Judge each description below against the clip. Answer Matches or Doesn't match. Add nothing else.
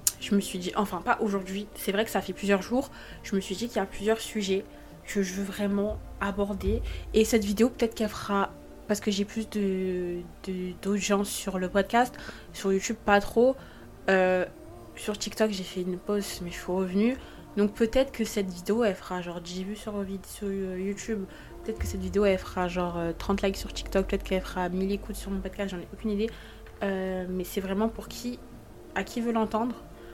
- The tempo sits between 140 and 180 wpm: Doesn't match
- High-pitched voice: Matches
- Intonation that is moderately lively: Doesn't match